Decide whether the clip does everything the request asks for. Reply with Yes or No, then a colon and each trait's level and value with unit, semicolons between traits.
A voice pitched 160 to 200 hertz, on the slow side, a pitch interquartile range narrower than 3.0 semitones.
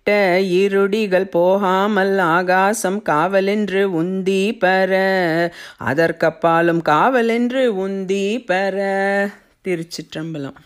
Yes: high, 190 Hz; slow, 60 wpm; narrow, 2.5 semitones